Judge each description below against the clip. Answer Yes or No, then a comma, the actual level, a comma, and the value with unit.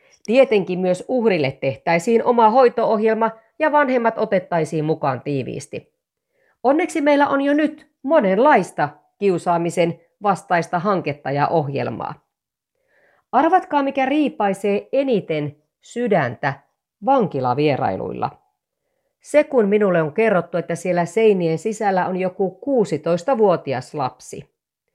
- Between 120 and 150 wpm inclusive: No, average, 100 wpm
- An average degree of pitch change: No, wide, 8.0 semitones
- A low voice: No, high, 200 Hz